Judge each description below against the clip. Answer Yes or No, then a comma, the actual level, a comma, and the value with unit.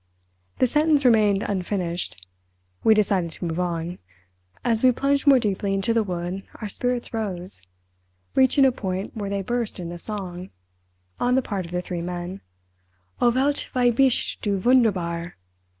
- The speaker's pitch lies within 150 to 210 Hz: Yes, high, 190 Hz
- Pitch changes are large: Yes, wide, 5.7 semitones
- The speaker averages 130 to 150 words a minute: Yes, average, 145 wpm